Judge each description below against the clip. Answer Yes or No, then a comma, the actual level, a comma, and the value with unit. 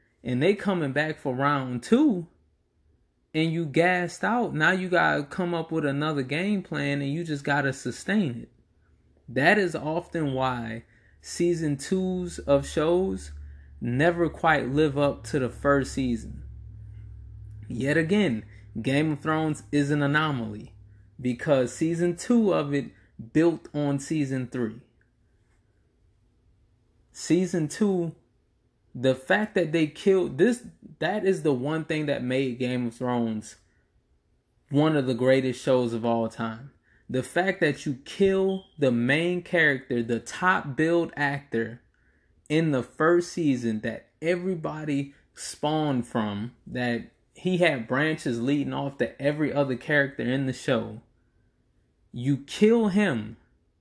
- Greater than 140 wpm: No, slow, 135 wpm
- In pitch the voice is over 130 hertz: Yes, medium, 140 Hz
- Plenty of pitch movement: Yes, wide, 5.8 semitones